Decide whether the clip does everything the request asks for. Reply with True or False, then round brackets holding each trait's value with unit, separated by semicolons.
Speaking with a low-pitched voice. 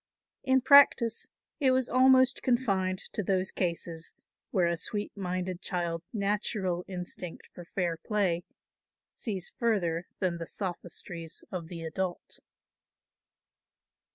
False (185 Hz)